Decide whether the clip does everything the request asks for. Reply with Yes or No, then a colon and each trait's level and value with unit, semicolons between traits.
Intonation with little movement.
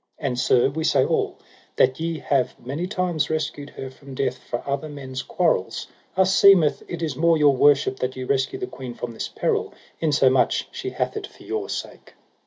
No: average, 4.2 semitones